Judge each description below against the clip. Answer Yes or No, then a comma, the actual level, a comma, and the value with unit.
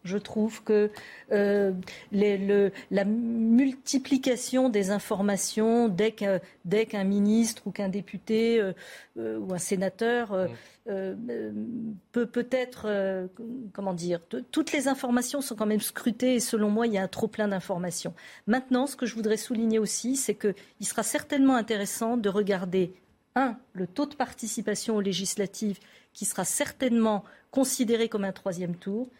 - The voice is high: Yes, high, 215 Hz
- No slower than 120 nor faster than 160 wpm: Yes, average, 155 wpm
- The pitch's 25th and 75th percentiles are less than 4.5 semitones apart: Yes, average, 3.3 semitones